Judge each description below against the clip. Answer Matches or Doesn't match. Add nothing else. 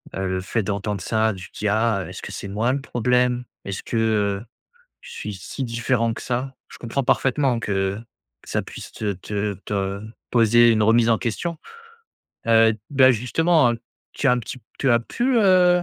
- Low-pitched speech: Matches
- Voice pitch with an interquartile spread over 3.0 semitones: Matches